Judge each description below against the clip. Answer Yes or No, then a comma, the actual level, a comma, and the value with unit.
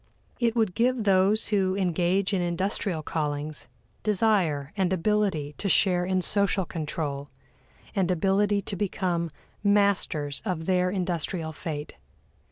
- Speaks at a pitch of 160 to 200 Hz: Yes, medium, 185 Hz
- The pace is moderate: No, slow, 125 wpm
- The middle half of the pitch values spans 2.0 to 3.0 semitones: No, average, 3.6 semitones